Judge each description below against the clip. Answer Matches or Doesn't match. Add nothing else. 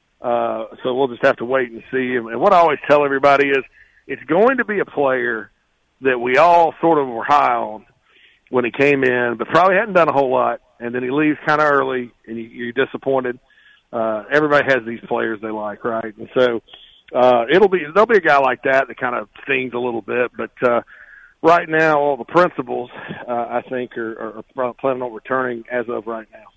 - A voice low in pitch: Matches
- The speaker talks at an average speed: Doesn't match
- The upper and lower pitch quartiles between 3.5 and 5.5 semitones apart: Doesn't match